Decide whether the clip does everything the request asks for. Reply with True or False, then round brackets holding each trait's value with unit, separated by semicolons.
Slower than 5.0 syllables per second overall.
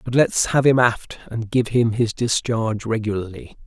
True (4.7 syllables/s)